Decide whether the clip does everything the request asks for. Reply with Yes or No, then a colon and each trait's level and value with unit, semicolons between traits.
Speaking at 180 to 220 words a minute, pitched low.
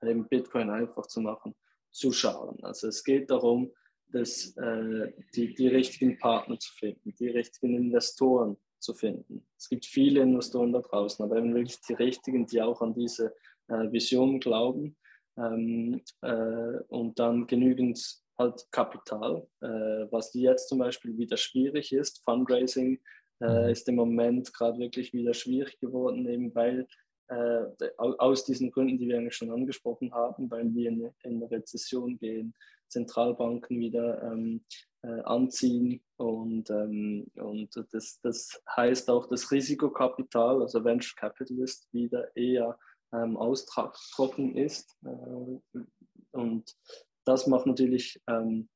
No: average, 140 wpm; low, 120 Hz